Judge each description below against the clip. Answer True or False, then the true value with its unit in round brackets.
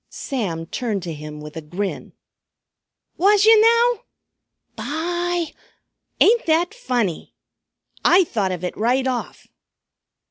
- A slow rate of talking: True (115 wpm)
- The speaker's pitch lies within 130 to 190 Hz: False (260 Hz)